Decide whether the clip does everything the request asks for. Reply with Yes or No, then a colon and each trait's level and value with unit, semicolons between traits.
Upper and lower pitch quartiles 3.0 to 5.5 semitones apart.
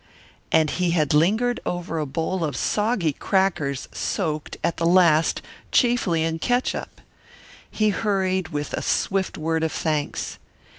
Yes: average, 3.8 semitones